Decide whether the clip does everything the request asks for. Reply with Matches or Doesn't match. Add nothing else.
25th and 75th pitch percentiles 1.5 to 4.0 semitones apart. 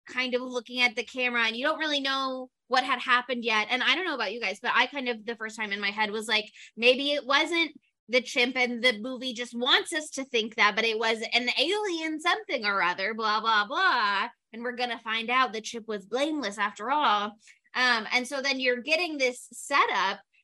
Matches